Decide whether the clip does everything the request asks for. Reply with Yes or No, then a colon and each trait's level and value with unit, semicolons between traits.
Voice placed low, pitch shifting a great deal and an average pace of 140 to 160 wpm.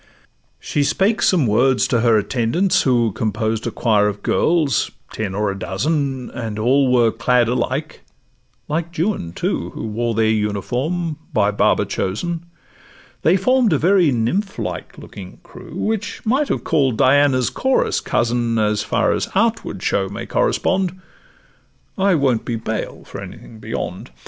Yes: low, 125 Hz; wide, 6.9 semitones; average, 150 wpm